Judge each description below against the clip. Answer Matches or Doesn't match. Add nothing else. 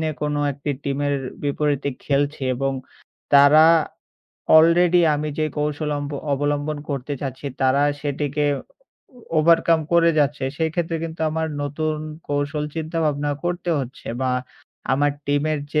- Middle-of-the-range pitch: Matches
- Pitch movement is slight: Matches